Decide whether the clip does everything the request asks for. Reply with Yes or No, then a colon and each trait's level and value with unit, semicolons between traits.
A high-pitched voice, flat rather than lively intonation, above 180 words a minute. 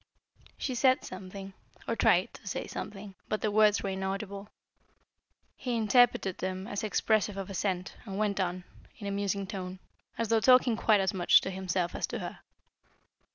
No: high, 200 Hz; narrow, 2.2 semitones; average, 170 wpm